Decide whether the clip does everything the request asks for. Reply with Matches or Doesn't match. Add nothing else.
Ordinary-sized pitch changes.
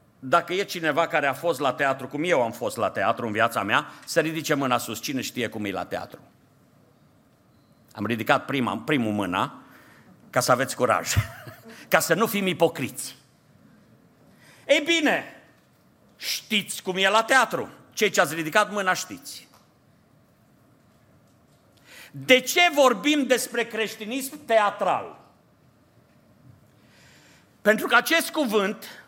Doesn't match